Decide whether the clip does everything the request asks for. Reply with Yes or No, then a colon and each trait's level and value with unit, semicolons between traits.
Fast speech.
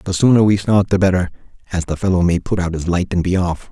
Yes: fast, 275 wpm